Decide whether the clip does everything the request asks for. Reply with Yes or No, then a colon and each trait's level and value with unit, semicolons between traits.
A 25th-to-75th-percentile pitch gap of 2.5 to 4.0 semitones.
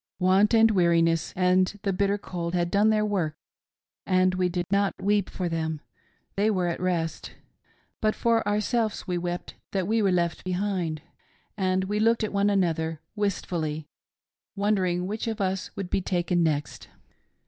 Yes: average, 2.9 semitones